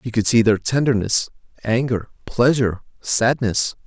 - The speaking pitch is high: No, low, 115 Hz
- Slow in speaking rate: Yes, slow, 125 wpm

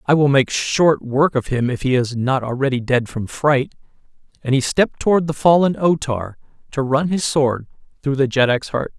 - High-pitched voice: No, low, 135 Hz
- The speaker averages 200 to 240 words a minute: Yes, fast, 205 wpm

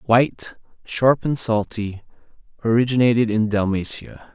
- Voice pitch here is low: Yes, low, 115 Hz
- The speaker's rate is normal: No, slow, 95 wpm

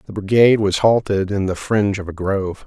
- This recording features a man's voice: Yes, male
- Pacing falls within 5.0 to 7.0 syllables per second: Yes, 6.0 syllables/s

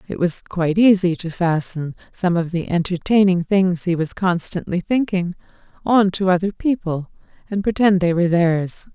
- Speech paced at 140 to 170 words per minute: Yes, average, 160 wpm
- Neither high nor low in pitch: Yes, medium, 180 Hz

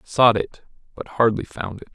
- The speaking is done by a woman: No, male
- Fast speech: No, average, 185 wpm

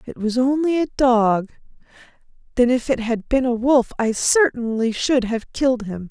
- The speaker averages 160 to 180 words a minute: Yes, average, 175 wpm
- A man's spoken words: No, female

